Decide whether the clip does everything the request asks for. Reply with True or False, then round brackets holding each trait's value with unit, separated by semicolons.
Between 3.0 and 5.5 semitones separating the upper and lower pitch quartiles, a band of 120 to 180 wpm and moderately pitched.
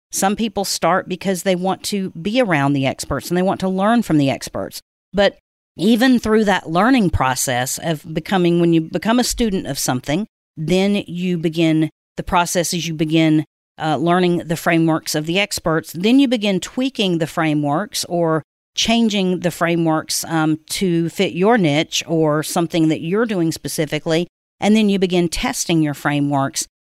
True (3.6 semitones; 170 wpm; 170 Hz)